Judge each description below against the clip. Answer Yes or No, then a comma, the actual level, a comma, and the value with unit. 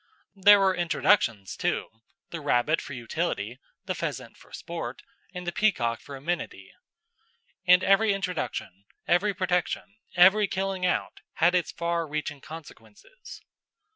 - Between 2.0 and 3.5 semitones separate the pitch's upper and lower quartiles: No, average, 5.3 semitones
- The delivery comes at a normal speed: No, slow, 130 wpm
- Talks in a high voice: No, medium, 175 Hz